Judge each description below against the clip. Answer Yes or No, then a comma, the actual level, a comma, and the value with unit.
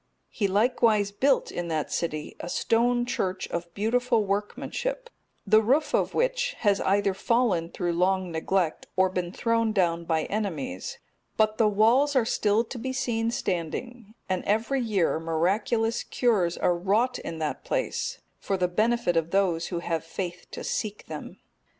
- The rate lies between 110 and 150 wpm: No, average, 160 wpm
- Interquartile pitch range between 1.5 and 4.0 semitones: No, average, 5.1 semitones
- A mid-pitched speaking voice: No, high, 205 Hz